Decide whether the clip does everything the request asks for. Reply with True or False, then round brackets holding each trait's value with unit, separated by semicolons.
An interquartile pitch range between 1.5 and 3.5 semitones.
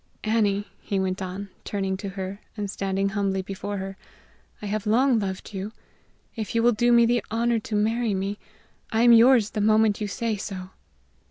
True (2.6 semitones)